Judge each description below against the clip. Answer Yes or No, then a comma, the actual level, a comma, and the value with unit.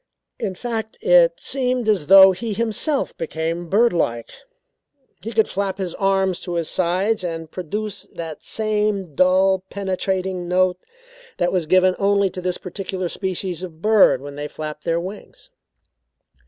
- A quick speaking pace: No, average, 145 wpm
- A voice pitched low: No, medium, 185 Hz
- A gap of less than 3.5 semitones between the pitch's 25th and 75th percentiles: Yes, average, 3.1 semitones